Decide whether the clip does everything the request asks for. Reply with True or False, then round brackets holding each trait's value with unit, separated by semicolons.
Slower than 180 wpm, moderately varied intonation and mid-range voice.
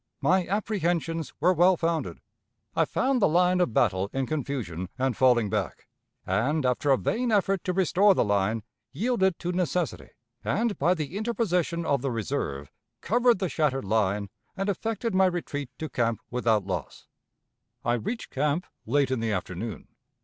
False (160 wpm; 7.9 semitones; 155 Hz)